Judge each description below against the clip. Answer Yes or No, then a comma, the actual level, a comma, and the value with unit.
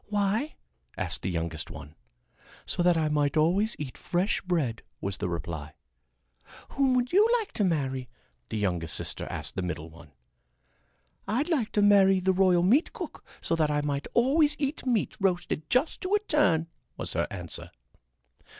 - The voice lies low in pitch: No, medium, 175 Hz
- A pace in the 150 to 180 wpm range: Yes, average, 170 wpm